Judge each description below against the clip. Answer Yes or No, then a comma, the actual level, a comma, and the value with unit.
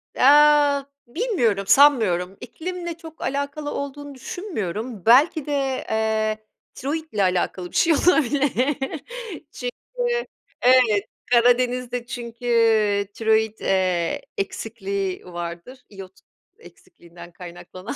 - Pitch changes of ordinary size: No, wide, 6.2 semitones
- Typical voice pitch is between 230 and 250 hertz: Yes, high, 240 Hz